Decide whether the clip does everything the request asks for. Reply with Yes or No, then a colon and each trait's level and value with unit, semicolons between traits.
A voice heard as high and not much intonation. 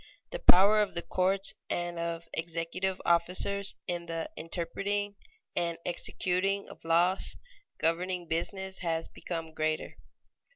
No: medium, 175 Hz; narrow, 2.3 semitones